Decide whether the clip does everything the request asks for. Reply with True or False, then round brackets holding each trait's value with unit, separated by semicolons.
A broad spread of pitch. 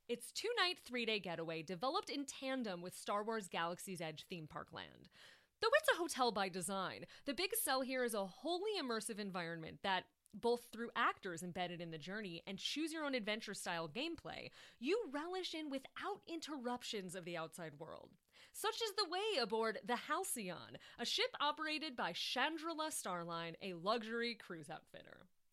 True (8.9 semitones)